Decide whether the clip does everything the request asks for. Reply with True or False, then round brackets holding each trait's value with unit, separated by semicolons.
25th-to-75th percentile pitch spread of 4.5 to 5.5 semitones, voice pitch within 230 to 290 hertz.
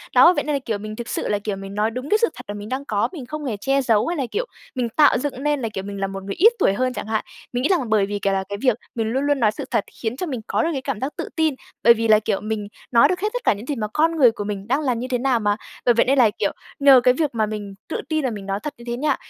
True (5.1 semitones; 240 Hz)